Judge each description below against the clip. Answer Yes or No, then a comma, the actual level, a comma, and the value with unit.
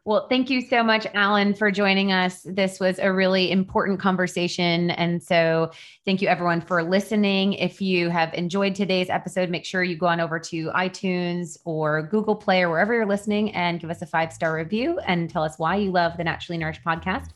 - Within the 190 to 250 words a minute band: Yes, fast, 205 wpm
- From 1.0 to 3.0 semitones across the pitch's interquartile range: Yes, narrow, 2.6 semitones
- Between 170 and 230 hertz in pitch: Yes, medium, 185 Hz